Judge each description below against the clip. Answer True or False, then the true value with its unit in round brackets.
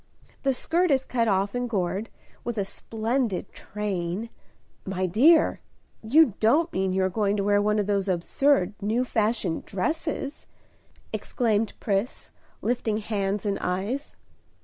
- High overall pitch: True (210 Hz)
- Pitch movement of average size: True (4.1 semitones)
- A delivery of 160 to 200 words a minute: False (145 wpm)